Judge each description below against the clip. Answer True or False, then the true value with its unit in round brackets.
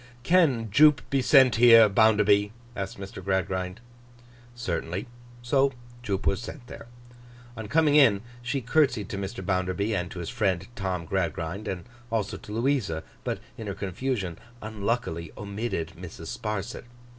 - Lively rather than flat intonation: False (4.2 semitones)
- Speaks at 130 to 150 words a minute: True (145 wpm)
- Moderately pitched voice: False (105 Hz)